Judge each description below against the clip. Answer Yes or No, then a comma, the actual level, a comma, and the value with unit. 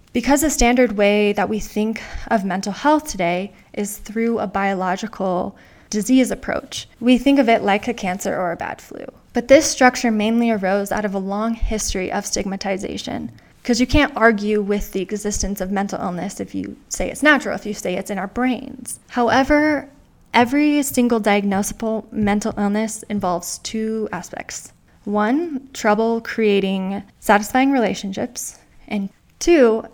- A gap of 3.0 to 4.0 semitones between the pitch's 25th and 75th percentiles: Yes, average, 3.4 semitones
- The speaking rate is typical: Yes, average, 155 wpm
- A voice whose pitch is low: No, high, 215 Hz